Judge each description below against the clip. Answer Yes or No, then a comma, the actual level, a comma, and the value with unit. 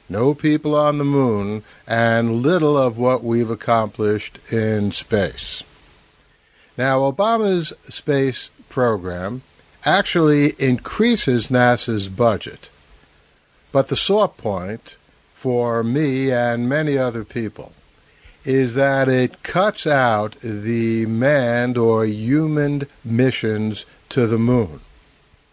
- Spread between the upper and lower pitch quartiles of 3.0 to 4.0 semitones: Yes, average, 3.7 semitones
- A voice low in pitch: Yes, low, 120 Hz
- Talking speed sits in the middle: No, slow, 105 wpm